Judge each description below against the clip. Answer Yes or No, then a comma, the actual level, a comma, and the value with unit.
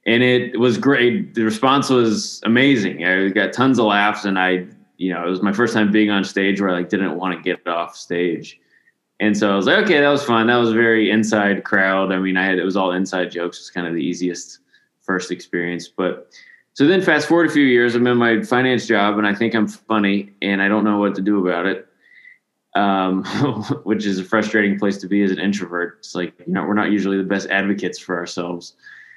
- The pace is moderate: No, fast, 240 wpm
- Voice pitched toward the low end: Yes, low, 100 Hz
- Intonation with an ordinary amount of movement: Yes, average, 3.4 semitones